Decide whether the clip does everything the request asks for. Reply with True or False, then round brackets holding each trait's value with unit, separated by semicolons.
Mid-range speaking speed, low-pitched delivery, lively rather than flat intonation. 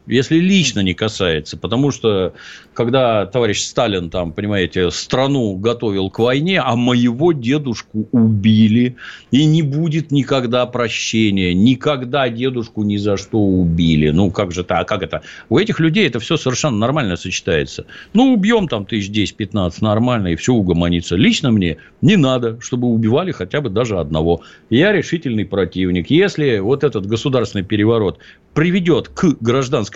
True (150 wpm; 115 Hz; 5.7 semitones)